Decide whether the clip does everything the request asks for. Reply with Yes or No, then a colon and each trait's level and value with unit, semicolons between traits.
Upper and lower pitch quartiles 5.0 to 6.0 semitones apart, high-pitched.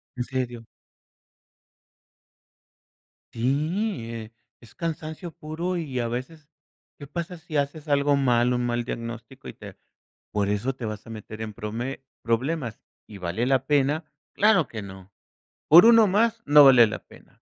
No: average, 5.3 semitones; low, 135 Hz